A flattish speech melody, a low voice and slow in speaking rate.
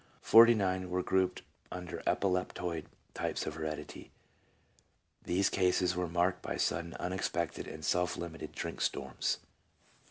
Yes: narrow, 1.8 semitones; very low, 90 Hz; slow, 130 wpm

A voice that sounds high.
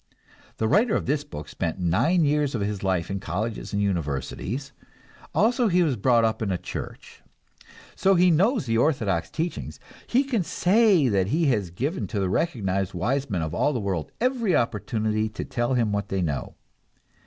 No: low, 115 Hz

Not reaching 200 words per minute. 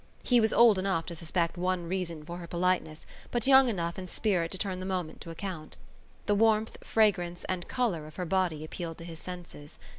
No: fast, 205 wpm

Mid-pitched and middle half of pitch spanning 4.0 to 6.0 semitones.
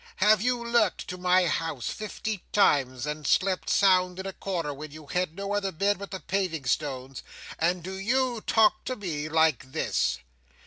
Yes: medium, 180 Hz; average, 4.9 semitones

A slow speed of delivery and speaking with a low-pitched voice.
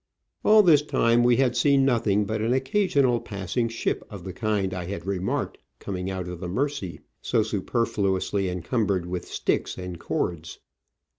No: average, 160 wpm; low, 105 Hz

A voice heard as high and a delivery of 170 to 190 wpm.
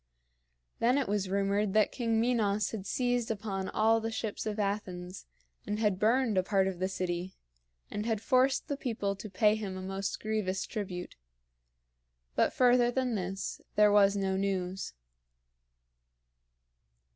No: high, 205 Hz; average, 150 wpm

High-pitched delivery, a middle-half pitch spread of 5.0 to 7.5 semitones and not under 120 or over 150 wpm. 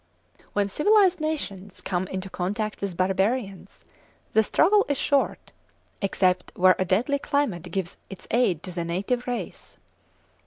Yes: high, 200 Hz; wide, 5.6 semitones; average, 140 wpm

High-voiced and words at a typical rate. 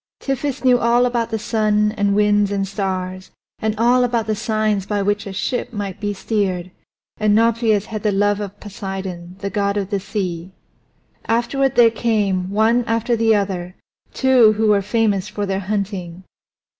Yes: high, 210 Hz; average, 170 wpm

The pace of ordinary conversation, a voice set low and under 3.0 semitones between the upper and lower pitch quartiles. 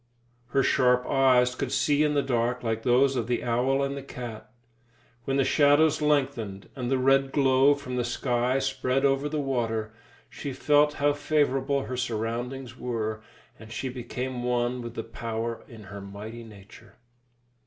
Yes: average, 165 wpm; low, 125 Hz; narrow, 2.6 semitones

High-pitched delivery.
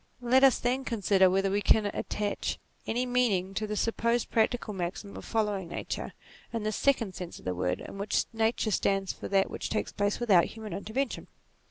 Yes: high, 210 Hz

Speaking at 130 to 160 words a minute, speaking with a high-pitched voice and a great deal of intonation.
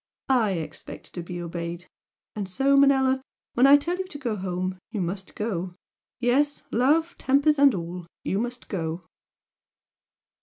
Yes: average, 150 wpm; high, 215 Hz; wide, 7.5 semitones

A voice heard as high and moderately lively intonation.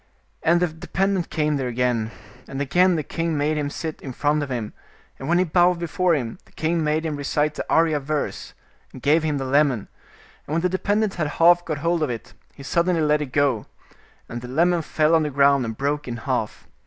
No: medium, 150 Hz; average, 3.3 semitones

